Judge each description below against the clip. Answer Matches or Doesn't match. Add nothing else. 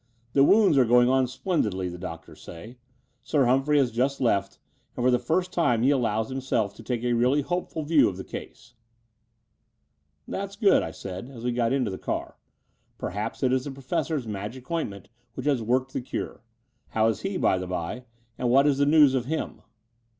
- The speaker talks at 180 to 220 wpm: Matches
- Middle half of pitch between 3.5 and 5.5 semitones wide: Matches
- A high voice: Doesn't match